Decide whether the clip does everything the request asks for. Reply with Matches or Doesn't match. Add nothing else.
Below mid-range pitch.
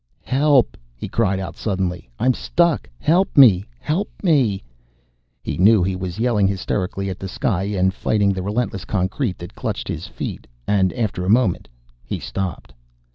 Matches